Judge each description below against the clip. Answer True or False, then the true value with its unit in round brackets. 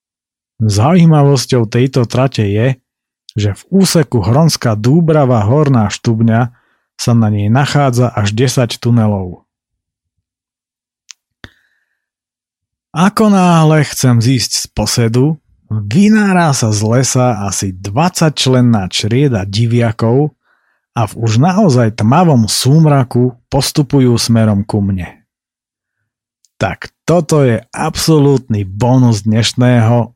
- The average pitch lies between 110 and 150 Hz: True (125 Hz)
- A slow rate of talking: True (95 wpm)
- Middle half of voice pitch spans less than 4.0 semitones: False (4.3 semitones)